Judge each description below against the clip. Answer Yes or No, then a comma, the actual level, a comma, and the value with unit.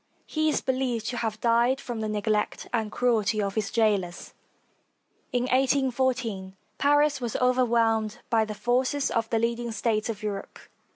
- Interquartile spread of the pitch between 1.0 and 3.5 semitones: Yes, average, 2.9 semitones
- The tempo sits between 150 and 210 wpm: Yes, average, 165 wpm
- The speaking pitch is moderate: No, high, 230 Hz